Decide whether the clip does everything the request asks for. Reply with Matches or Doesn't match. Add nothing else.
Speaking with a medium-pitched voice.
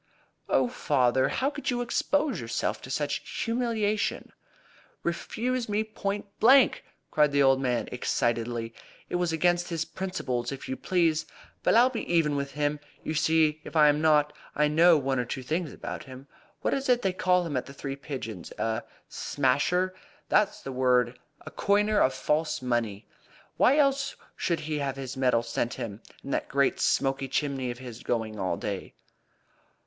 Matches